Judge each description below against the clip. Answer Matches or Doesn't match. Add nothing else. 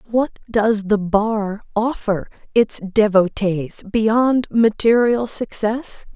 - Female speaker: Matches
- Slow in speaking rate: Matches